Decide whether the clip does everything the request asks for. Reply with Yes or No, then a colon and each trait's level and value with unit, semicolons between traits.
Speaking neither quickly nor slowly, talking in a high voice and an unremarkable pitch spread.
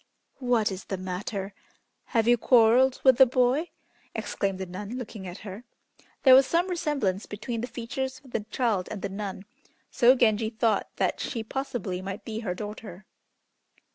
Yes: average, 170 wpm; high, 225 Hz; average, 4.2 semitones